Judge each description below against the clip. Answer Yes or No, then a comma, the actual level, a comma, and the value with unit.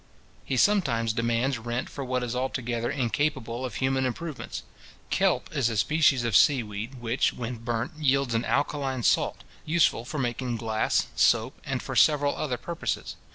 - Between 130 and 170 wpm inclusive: Yes, average, 160 wpm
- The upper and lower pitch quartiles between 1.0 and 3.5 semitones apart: Yes, average, 3.0 semitones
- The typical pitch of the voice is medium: No, low, 125 Hz